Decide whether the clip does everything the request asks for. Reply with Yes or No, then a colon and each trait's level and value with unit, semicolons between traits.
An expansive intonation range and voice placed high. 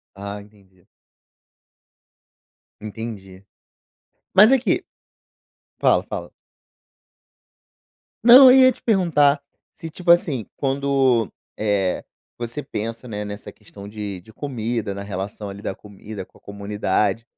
No: wide, 5.7 semitones; low, 110 Hz